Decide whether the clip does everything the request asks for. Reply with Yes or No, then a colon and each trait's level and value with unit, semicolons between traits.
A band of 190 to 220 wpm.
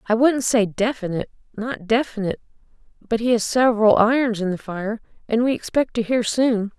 No: average, 175 wpm